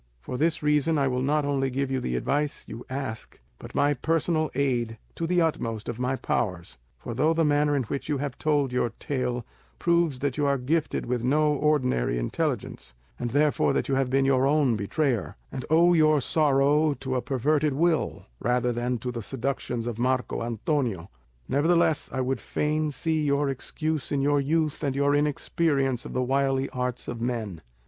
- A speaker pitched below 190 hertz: Yes, low, 135 Hz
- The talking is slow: No, average, 185 wpm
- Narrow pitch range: No, average, 3.2 semitones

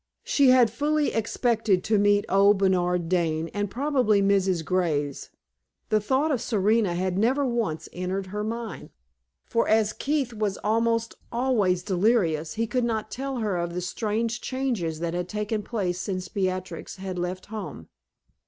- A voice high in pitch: Yes, high, 205 Hz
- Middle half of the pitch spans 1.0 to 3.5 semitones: No, average, 4.1 semitones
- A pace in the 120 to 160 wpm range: Yes, average, 155 wpm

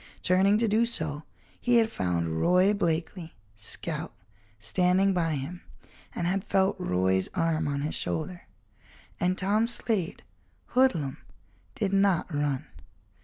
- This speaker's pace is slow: Yes, slow, 125 wpm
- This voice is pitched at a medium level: Yes, medium, 180 Hz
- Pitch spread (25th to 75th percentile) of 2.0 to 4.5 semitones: No, average, 5.1 semitones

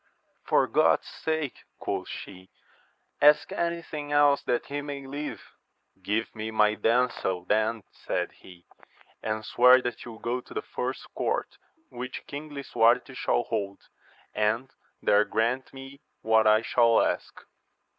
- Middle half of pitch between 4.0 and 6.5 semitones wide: Yes, average, 4.6 semitones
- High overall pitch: No, low, 120 Hz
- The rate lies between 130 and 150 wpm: Yes, average, 145 wpm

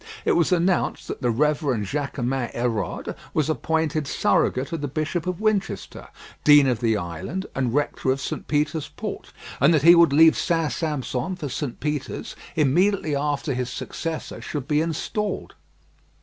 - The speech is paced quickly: No, average, 160 wpm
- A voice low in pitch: No, medium, 150 Hz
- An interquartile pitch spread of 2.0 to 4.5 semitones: Yes, average, 3.8 semitones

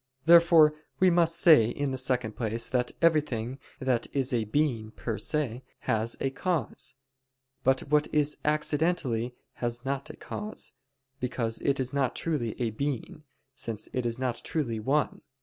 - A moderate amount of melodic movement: Yes, average, 4.4 semitones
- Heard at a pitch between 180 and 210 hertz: No, low, 130 Hz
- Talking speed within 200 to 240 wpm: No, average, 155 wpm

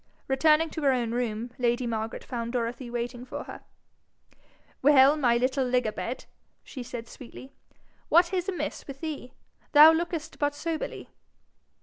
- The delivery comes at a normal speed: Yes, average, 150 wpm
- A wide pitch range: No, average, 4.2 semitones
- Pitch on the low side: No, very high, 260 Hz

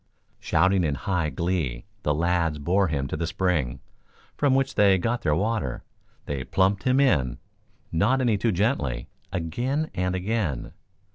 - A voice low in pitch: Yes, very low, 90 Hz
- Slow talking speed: No, average, 150 wpm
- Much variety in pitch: Yes, wide, 6.3 semitones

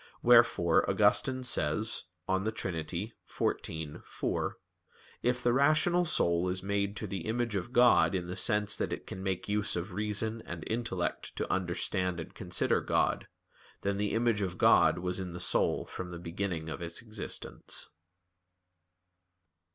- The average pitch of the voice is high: No, low, 100 Hz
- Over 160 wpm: No, average, 150 wpm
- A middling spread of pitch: Yes, average, 4.3 semitones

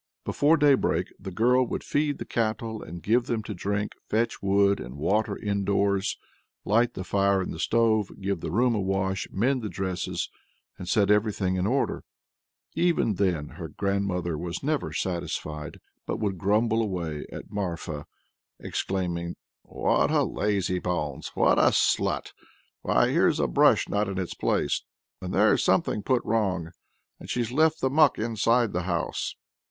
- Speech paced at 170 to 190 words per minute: No, average, 160 wpm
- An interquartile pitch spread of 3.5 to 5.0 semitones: Yes, average, 3.8 semitones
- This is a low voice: Yes, low, 100 Hz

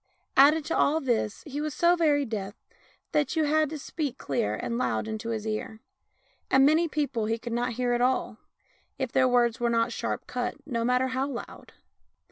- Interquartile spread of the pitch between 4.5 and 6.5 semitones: No, average, 4.1 semitones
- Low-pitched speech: No, very high, 250 Hz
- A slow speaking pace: No, average, 195 wpm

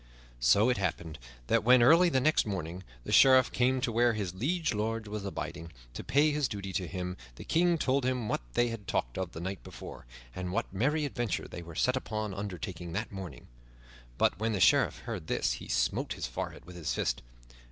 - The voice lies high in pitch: No, low, 105 Hz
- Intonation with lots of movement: Yes, wide, 5.9 semitones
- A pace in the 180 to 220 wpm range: Yes, fast, 205 wpm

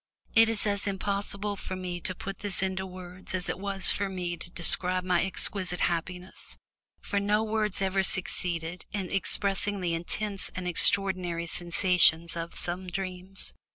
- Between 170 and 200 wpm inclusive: No, average, 155 wpm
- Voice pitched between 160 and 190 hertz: Yes, medium, 185 Hz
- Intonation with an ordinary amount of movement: No, narrow, 1.9 semitones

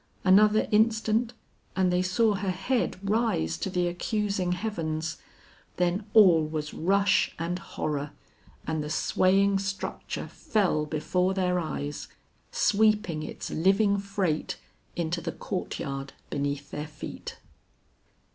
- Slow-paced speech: Yes, slow, 120 wpm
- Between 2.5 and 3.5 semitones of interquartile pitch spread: No, average, 4.2 semitones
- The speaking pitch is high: No, medium, 180 Hz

